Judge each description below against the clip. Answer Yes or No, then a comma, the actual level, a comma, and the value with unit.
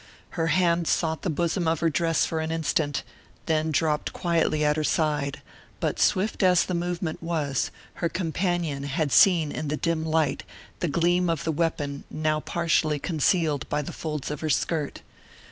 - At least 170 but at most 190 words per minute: Yes, average, 175 wpm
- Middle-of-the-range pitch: Yes, medium, 160 Hz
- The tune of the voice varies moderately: No, narrow, 2.1 semitones